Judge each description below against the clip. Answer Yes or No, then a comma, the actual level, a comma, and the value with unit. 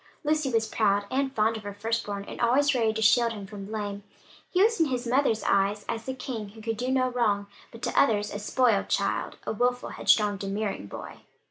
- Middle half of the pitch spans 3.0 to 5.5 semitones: Yes, average, 3.5 semitones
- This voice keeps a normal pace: No, fast, 220 wpm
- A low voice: No, high, 225 Hz